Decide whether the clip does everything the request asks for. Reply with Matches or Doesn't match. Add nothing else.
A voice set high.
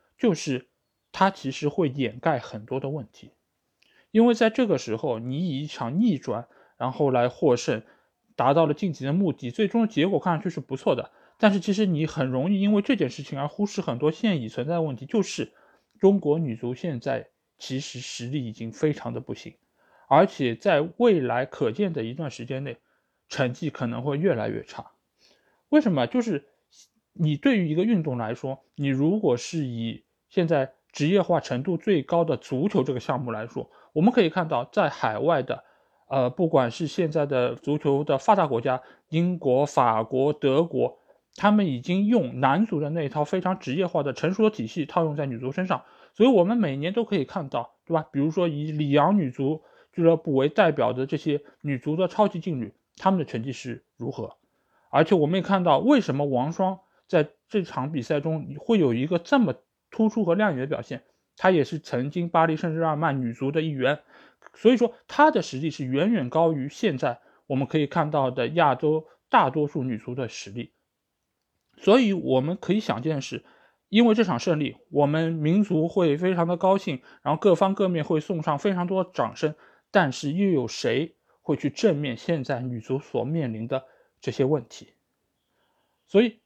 Doesn't match